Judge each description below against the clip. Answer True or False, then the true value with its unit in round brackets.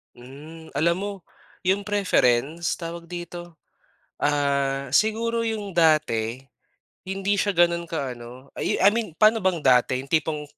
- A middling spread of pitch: False (5.8 semitones)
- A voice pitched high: False (165 Hz)